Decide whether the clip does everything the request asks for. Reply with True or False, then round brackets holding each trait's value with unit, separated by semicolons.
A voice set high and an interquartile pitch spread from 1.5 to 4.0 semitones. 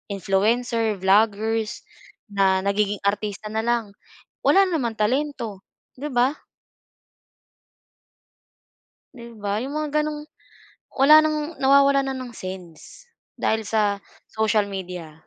False (220 Hz; 5.2 semitones)